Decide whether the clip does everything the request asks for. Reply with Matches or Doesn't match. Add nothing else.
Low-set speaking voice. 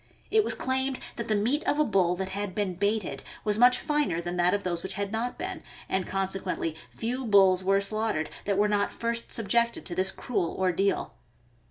Doesn't match